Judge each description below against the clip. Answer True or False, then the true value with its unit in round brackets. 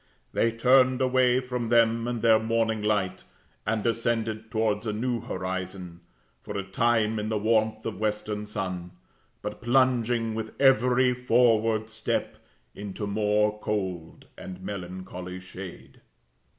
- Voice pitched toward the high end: False (110 Hz)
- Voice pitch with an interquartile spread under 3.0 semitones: True (2.4 semitones)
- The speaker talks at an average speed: False (130 wpm)